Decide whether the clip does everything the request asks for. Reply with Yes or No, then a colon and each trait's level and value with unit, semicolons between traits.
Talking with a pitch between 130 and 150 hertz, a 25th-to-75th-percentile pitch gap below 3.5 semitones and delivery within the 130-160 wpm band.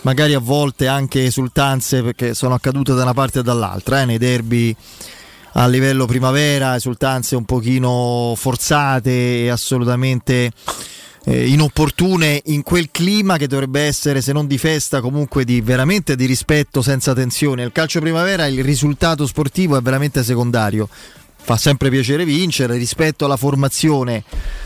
Yes: low, 135 Hz; average, 2.7 semitones; average, 145 wpm